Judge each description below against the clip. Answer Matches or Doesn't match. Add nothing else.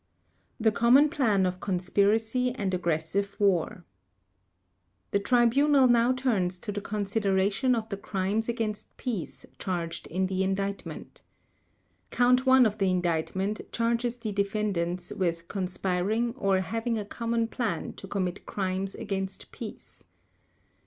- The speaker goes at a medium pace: Doesn't match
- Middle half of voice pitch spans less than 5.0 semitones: Matches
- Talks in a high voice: Matches